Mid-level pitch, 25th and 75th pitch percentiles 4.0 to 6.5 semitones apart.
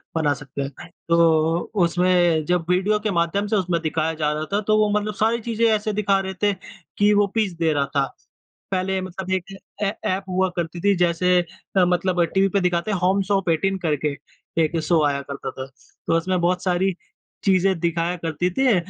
No: medium, 180 Hz; average, 2.9 semitones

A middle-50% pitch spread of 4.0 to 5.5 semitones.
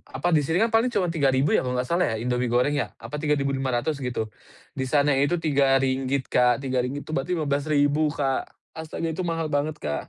No: average, 2.9 semitones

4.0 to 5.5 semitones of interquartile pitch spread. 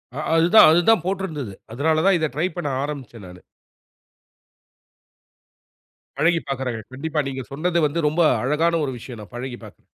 Yes: average, 4.3 semitones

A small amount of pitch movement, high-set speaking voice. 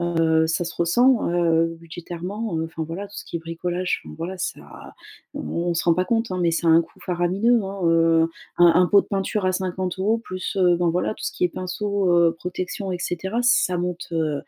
No: narrow, 2.3 semitones; medium, 175 Hz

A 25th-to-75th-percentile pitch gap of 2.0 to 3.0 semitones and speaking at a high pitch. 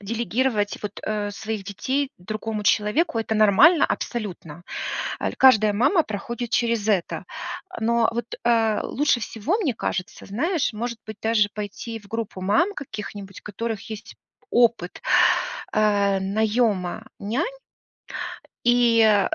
Yes: narrow, 2.6 semitones; high, 220 Hz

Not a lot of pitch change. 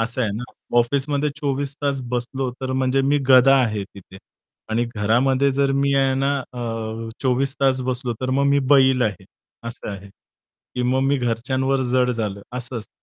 Yes: narrow, 2.3 semitones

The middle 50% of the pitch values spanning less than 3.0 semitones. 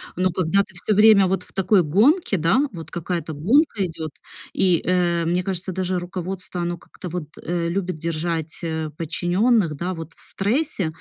Yes: narrow, 2.5 semitones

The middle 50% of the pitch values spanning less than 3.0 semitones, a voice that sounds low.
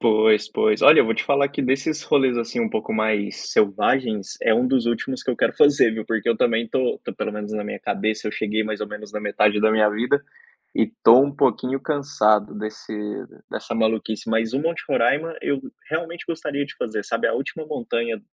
No: average, 4.2 semitones; low, 115 Hz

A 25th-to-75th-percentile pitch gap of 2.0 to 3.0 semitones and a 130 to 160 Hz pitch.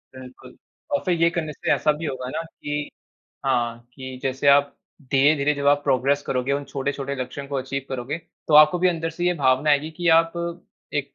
Yes: average, 2.7 semitones; medium, 140 Hz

